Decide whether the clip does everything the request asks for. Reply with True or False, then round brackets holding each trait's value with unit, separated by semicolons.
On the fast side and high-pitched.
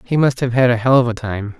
False (340 wpm; 120 Hz)